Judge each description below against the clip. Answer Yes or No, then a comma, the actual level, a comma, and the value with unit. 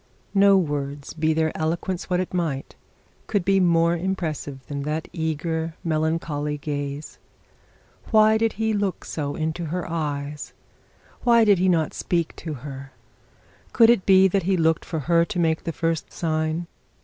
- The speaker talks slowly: No, average, 155 wpm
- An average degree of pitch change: Yes, average, 3.4 semitones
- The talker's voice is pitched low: No, medium, 165 Hz